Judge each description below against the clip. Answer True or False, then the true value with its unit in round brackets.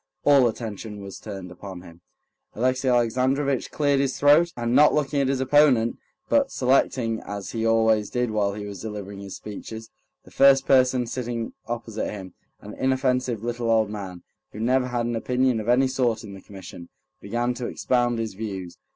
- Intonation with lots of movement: False (3.6 semitones)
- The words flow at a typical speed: True (175 wpm)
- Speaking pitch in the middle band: False (120 Hz)